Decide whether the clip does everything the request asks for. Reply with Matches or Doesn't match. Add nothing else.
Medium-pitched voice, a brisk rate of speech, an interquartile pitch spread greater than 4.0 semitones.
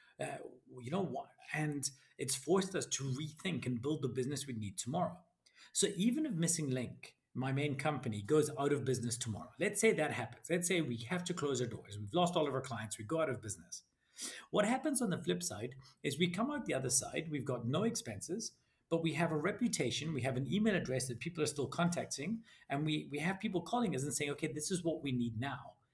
Matches